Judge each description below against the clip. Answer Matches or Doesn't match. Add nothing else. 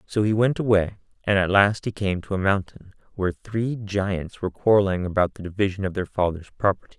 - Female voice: Doesn't match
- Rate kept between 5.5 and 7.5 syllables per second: Matches